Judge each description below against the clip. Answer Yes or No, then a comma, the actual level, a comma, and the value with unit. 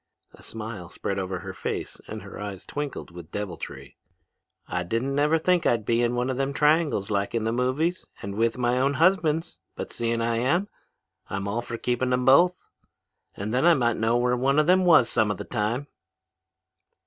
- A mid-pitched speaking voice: No, low, 120 Hz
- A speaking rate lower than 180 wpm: No, average, 195 wpm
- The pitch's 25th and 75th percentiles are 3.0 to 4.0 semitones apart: No, average, 5.1 semitones